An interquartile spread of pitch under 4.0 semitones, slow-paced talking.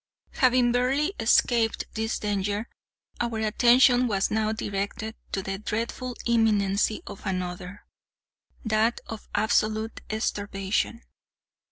Yes: narrow, 2.6 semitones; slow, 95 wpm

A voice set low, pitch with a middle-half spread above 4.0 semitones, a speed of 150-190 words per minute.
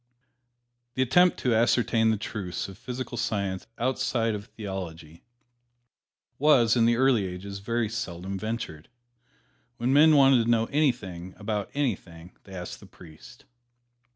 No: low, 110 Hz; average, 4.6 semitones; slow, 135 wpm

